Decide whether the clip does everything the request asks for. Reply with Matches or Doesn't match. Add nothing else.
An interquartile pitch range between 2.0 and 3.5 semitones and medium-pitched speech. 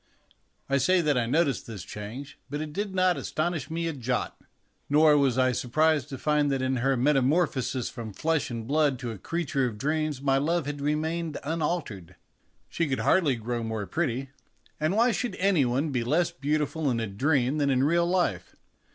Doesn't match